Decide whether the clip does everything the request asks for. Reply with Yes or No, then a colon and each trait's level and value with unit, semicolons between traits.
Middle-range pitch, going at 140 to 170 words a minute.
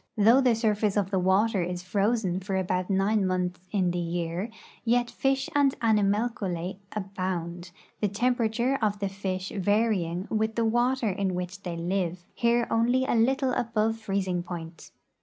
No: high, 200 Hz; average, 160 wpm